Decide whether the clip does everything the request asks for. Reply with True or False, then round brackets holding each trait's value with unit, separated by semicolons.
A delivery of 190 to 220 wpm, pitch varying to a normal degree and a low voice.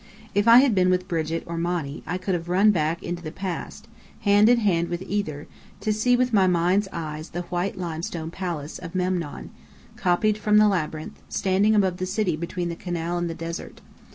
False (200 wpm; 3.2 semitones; 180 Hz)